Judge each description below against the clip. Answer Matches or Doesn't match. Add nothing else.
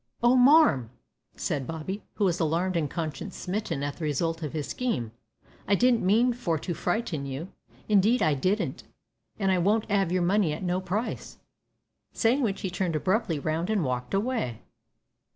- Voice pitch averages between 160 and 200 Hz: Matches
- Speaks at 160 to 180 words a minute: Matches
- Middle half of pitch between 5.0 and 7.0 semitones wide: Matches